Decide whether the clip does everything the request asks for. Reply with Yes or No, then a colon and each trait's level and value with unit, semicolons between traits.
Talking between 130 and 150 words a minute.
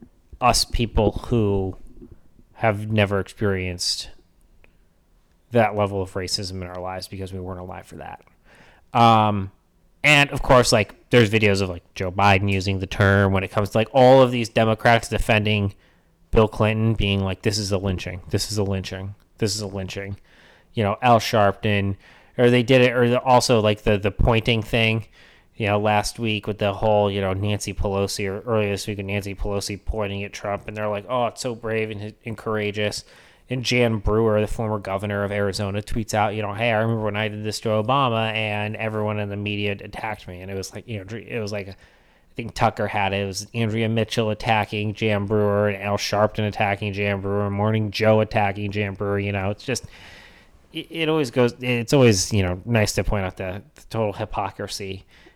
No: average, 200 wpm